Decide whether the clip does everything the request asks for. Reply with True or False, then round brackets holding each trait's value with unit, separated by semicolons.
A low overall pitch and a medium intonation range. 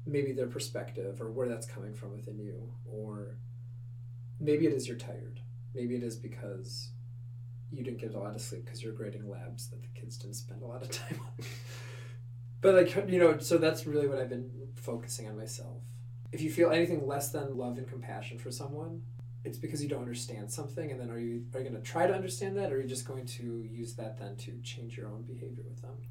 False (120 Hz; 1.3 semitones)